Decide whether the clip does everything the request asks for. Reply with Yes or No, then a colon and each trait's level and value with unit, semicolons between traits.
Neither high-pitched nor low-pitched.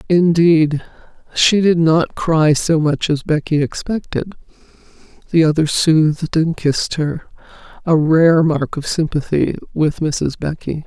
Yes: medium, 160 Hz